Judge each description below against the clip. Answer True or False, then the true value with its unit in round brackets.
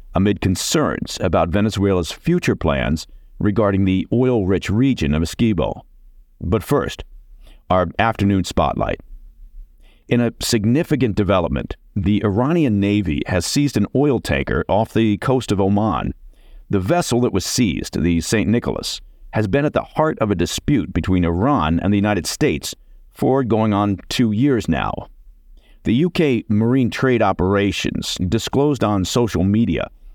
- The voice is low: True (100 Hz)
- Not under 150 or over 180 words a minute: False (140 wpm)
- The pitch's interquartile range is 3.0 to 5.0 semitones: False (5.5 semitones)